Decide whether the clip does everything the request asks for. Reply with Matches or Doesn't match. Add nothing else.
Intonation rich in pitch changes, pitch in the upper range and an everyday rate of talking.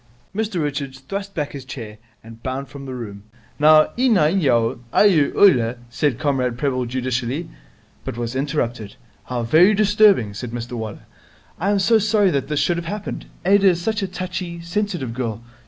Doesn't match